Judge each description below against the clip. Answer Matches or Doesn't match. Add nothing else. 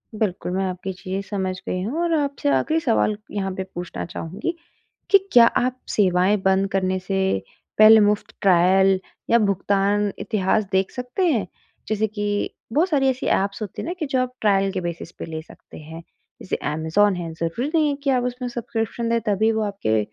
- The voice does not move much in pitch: Doesn't match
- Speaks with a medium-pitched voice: Doesn't match